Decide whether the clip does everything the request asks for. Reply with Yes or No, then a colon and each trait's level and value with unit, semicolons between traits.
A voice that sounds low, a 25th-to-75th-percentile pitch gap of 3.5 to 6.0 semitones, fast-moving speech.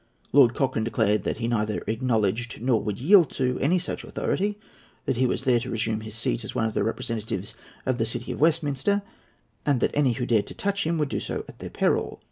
Yes: low, 120 Hz; average, 4.3 semitones; fast, 225 wpm